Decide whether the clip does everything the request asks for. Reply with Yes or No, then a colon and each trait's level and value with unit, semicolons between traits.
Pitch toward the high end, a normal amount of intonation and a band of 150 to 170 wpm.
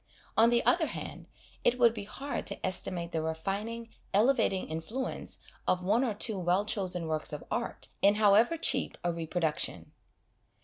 Yes: high, 200 Hz; average, 5.0 semitones; average, 160 wpm